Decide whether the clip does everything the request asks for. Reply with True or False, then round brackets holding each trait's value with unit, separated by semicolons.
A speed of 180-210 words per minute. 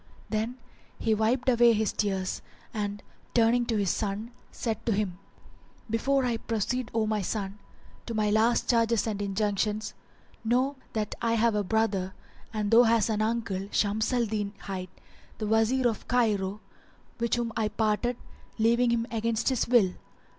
False (160 wpm)